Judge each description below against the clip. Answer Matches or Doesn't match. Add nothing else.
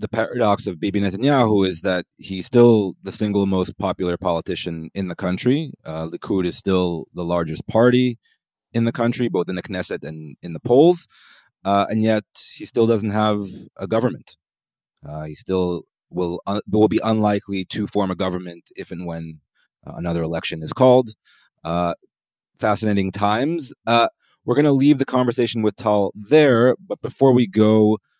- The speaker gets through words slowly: Doesn't match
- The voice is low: Matches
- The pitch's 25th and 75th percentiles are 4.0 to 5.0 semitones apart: Matches